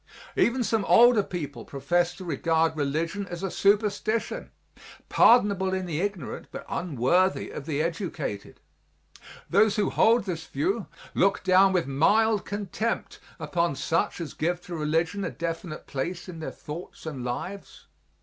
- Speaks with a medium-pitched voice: Yes, medium, 175 Hz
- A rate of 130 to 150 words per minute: Yes, average, 145 wpm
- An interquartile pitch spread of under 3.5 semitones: No, average, 4.0 semitones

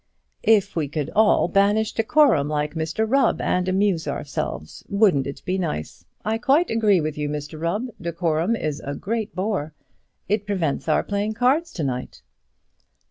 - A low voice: No, medium, 185 Hz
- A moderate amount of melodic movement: No, wide, 6.1 semitones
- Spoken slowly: No, average, 160 wpm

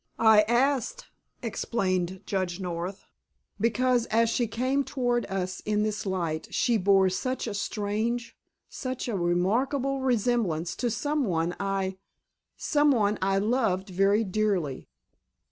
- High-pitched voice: Yes, high, 210 Hz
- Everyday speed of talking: No, slow, 115 wpm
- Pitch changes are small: No, average, 4.4 semitones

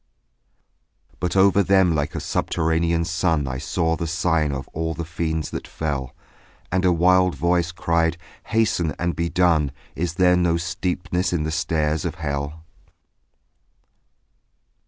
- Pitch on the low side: Yes, very low, 85 Hz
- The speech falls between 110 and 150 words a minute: Yes, average, 140 wpm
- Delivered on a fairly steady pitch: Yes, narrow, 2.1 semitones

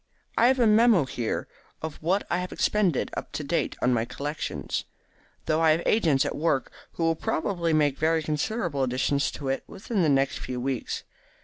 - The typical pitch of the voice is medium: Yes, medium, 155 Hz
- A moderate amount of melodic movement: Yes, average, 4.8 semitones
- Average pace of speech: Yes, average, 190 wpm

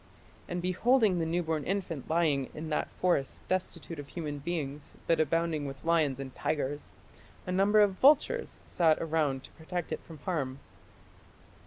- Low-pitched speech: No, medium, 165 Hz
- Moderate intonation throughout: Yes, average, 3.7 semitones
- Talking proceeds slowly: No, average, 155 wpm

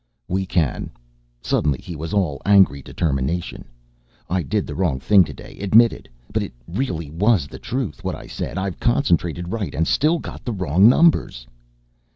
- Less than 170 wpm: Yes, average, 160 wpm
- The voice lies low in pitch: Yes, very low, 90 Hz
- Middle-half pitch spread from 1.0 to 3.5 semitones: No, average, 4.8 semitones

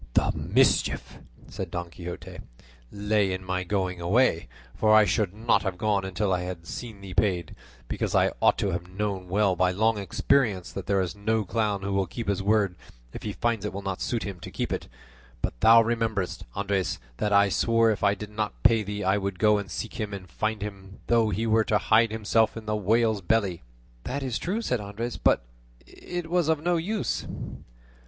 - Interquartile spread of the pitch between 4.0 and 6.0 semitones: No, average, 2.8 semitones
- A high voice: No, low, 105 Hz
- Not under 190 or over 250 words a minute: Yes, fast, 205 wpm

